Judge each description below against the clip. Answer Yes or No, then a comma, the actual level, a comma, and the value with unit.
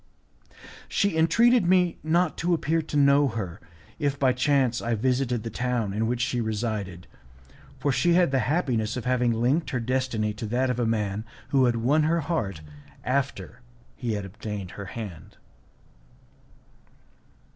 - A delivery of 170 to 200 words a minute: No, average, 155 wpm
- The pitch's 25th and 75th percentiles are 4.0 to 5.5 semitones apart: Yes, average, 4.8 semitones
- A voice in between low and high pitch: No, low, 125 Hz